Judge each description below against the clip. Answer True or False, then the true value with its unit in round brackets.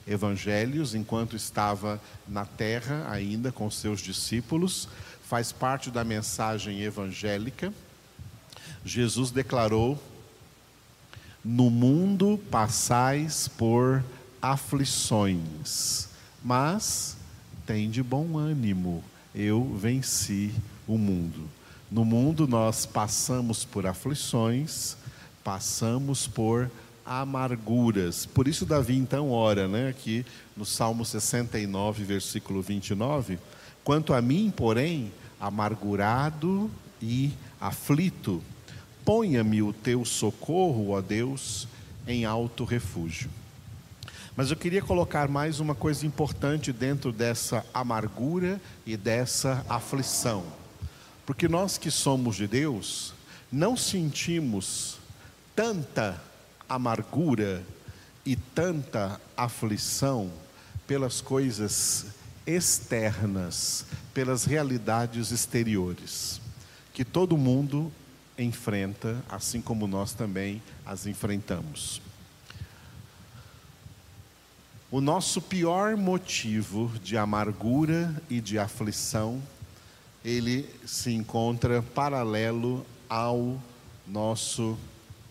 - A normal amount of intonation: True (4.0 semitones)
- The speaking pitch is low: True (120 Hz)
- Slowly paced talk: True (90 wpm)